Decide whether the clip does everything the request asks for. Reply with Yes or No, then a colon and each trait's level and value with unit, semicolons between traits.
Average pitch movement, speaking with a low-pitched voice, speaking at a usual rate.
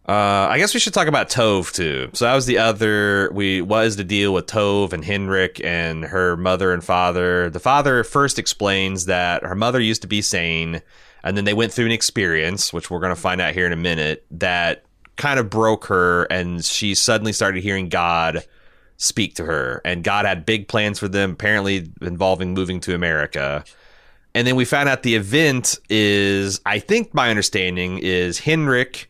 Yes: average, 3.7 semitones; low, 100 Hz; average, 195 wpm